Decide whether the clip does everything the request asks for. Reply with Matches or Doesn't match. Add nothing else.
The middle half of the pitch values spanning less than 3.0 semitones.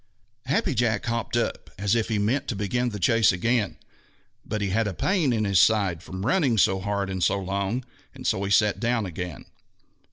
Doesn't match